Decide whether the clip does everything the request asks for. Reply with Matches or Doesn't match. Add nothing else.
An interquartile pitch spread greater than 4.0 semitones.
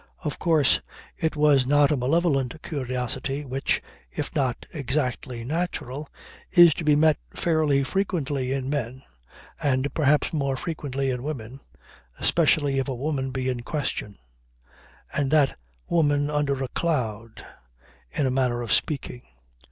Doesn't match